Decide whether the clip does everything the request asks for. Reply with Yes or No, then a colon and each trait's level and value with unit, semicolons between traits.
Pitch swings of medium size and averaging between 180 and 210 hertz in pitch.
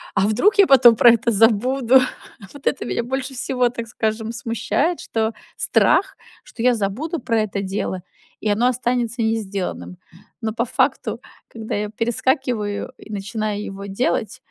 No: average, 3.1 semitones; high, 230 Hz